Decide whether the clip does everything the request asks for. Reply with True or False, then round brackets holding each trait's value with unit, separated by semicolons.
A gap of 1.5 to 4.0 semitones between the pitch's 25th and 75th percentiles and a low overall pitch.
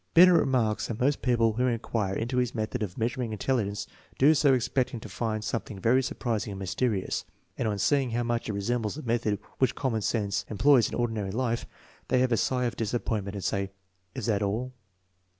True (3.3 semitones; 115 Hz)